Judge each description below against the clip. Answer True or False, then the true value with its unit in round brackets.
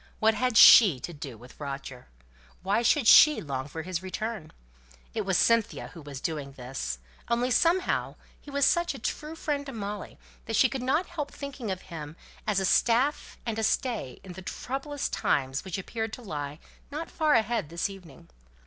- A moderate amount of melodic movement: False (8.8 semitones)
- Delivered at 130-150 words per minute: False (185 wpm)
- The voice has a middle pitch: False (210 Hz)